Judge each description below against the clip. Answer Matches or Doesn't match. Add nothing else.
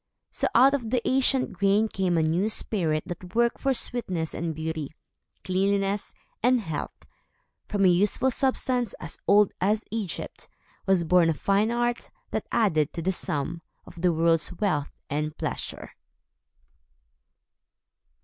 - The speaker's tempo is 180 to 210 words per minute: Doesn't match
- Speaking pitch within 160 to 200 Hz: Matches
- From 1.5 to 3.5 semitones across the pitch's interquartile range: Doesn't match